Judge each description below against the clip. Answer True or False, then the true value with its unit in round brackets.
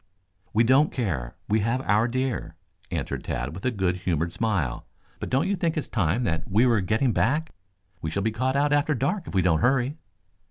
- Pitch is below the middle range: True (115 Hz)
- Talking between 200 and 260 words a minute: True (205 wpm)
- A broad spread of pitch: True (6.4 semitones)